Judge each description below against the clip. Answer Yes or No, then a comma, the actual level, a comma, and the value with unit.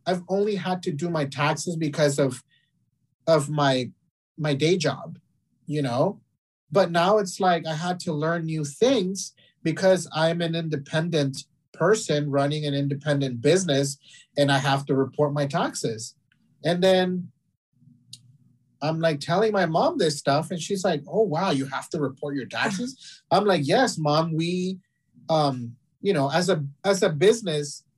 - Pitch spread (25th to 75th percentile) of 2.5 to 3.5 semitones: No, average, 4.1 semitones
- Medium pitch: Yes, medium, 155 Hz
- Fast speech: No, average, 160 wpm